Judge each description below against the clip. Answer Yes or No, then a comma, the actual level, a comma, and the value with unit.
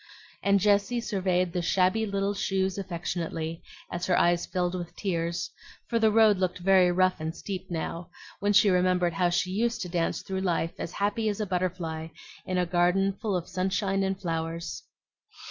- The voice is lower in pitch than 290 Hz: Yes, medium, 185 Hz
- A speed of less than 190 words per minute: Yes, average, 180 wpm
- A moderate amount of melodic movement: No, narrow, 2.2 semitones